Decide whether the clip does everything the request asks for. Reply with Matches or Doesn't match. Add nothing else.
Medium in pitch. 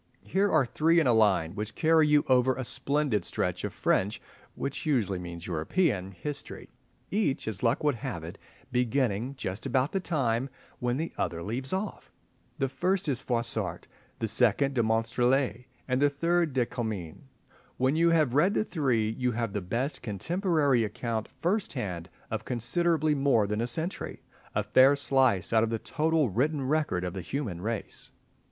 Doesn't match